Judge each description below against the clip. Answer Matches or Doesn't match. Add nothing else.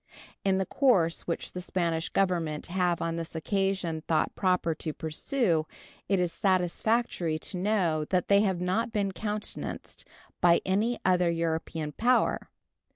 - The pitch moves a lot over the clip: Doesn't match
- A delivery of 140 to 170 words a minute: Matches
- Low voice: Doesn't match